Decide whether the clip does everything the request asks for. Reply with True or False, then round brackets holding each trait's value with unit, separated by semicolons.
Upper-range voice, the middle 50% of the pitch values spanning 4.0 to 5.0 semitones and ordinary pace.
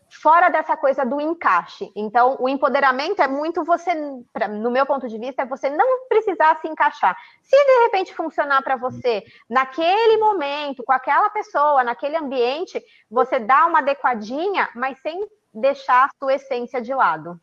True (285 Hz; 4.7 semitones; 160 wpm)